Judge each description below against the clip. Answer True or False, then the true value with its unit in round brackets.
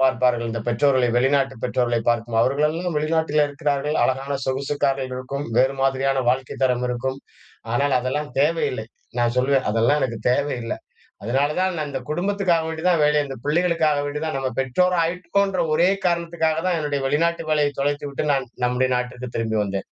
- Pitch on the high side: False (140 Hz)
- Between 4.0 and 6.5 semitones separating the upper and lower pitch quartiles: False (3.5 semitones)